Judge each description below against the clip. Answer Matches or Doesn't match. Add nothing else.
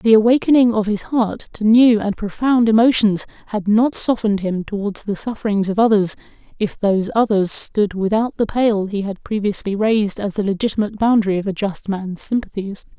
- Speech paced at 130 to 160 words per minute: Doesn't match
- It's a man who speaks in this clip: Doesn't match